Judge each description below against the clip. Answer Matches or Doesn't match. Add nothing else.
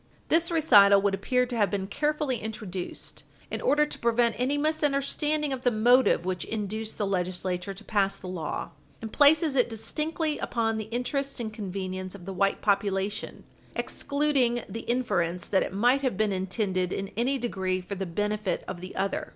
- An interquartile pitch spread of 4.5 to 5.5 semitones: Matches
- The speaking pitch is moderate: Doesn't match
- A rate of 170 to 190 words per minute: Matches